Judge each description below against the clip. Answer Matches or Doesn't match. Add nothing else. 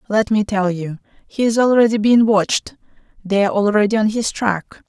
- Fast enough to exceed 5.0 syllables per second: Matches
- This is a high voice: Matches